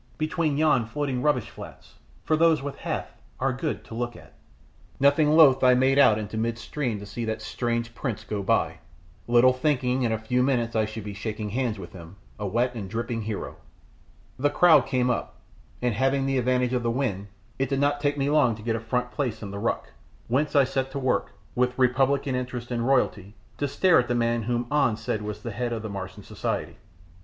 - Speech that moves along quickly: Yes, fast, 210 wpm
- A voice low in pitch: Yes, low, 125 Hz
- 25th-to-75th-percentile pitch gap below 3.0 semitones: No, average, 3.4 semitones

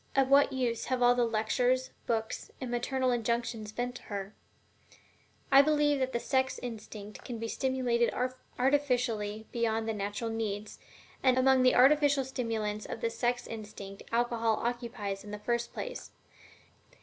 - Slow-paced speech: No, average, 150 wpm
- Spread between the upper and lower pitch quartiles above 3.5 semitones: No, average, 2.7 semitones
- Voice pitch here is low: No, high, 240 Hz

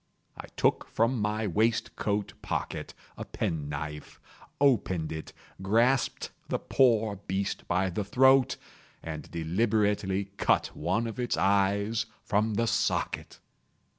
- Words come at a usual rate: No, slow, 120 wpm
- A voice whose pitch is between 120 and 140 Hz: No, low, 105 Hz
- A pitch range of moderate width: Yes, average, 3.3 semitones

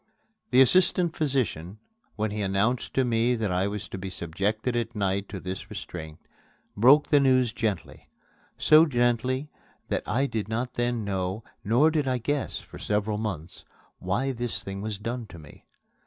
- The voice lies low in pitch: Yes, low, 110 Hz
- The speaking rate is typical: Yes, average, 170 wpm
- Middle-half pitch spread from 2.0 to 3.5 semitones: No, average, 4.6 semitones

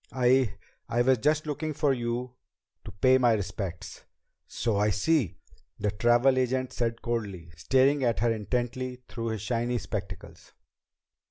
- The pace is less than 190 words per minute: Yes, average, 145 wpm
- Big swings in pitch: No, average, 3.7 semitones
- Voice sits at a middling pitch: No, low, 120 Hz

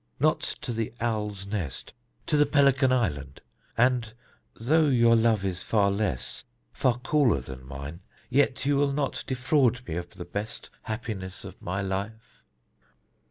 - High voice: No, low, 110 Hz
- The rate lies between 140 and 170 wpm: Yes, average, 150 wpm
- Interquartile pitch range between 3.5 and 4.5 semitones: No, average, 5.2 semitones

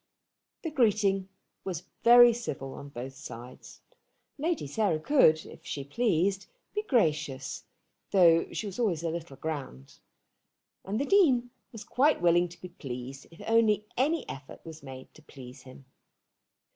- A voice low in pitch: No, medium, 175 Hz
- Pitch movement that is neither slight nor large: No, wide, 8.6 semitones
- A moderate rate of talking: Yes, average, 145 wpm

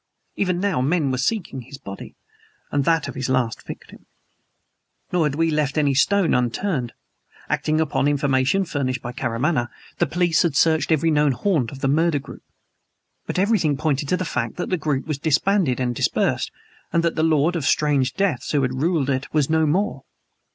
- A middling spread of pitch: Yes, average, 4.0 semitones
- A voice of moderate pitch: Yes, medium, 150 Hz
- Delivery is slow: No, average, 185 wpm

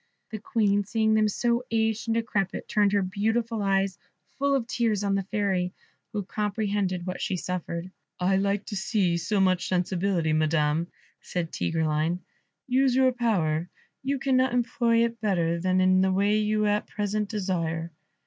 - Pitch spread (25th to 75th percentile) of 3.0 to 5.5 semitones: Yes, average, 3.4 semitones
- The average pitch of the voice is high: Yes, high, 200 Hz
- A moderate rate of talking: Yes, average, 160 wpm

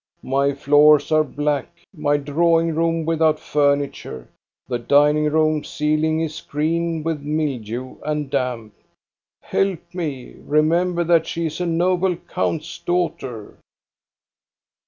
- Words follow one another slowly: Yes, slow, 115 wpm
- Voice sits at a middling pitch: Yes, medium, 155 Hz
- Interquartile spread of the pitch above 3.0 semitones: No, narrow, 2.5 semitones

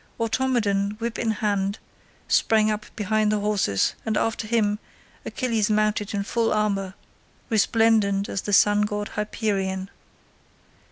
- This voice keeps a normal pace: No, slow, 125 wpm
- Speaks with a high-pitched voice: Yes, high, 210 Hz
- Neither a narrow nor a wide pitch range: No, narrow, 1.7 semitones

